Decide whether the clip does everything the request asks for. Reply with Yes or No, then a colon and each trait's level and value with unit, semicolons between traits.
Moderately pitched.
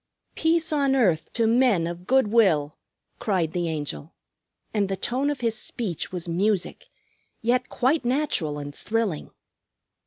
No: high, 215 Hz